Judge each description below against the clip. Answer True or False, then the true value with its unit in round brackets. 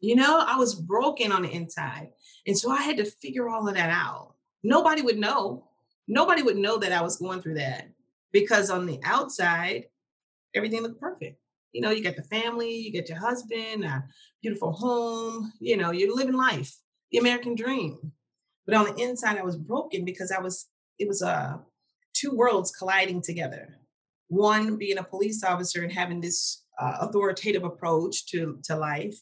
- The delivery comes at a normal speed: True (185 wpm)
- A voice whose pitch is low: False (200 Hz)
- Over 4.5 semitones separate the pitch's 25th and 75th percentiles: True (5.0 semitones)